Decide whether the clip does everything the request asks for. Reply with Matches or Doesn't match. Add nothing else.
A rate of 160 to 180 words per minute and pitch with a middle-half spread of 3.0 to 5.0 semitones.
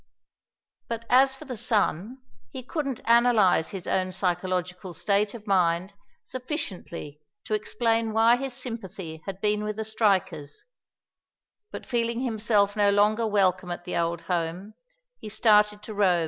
Doesn't match